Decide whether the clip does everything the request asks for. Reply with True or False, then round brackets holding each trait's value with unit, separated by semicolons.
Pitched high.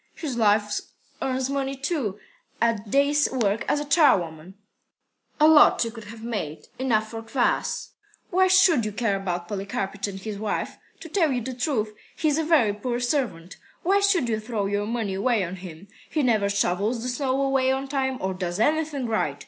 True (235 Hz)